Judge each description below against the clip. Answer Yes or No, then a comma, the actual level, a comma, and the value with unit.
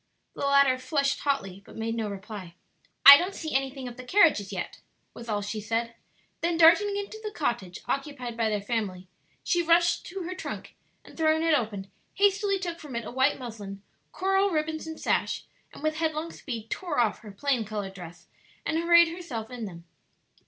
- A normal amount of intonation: No, wide, 7.4 semitones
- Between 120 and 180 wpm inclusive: No, average, 190 wpm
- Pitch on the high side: Yes, very high, 270 Hz